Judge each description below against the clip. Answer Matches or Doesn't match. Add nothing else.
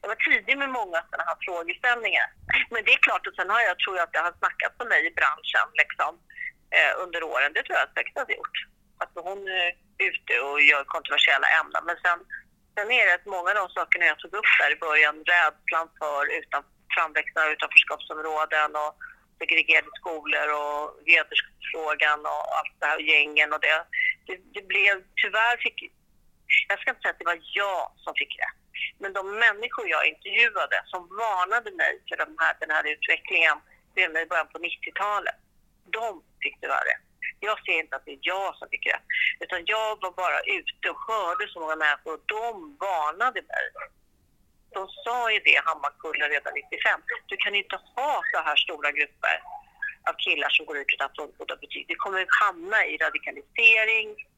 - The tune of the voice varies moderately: Doesn't match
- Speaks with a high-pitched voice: Matches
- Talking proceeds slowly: Doesn't match